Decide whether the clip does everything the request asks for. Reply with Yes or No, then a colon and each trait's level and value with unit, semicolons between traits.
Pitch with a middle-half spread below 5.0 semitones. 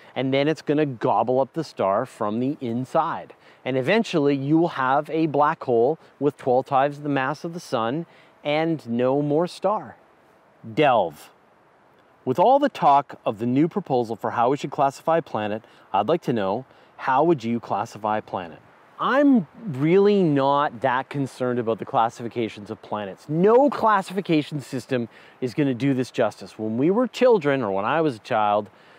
No: average, 5.3 semitones